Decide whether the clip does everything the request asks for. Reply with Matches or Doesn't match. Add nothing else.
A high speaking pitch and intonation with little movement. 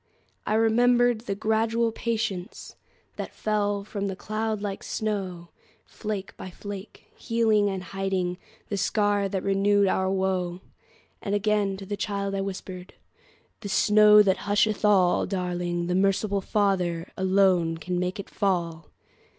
Matches